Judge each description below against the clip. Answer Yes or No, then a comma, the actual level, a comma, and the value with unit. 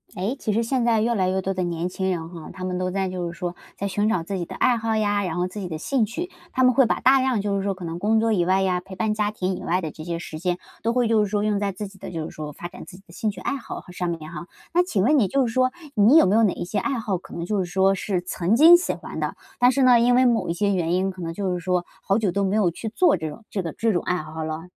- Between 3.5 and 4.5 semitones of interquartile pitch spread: Yes, average, 4.0 semitones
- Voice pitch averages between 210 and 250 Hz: No, high, 195 Hz